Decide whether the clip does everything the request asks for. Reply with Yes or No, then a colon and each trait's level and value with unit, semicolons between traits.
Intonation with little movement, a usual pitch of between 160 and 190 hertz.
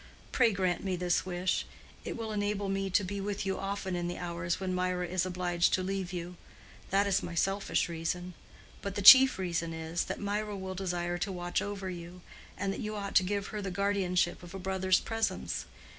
Yes: narrow, 2.1 semitones; medium, 185 Hz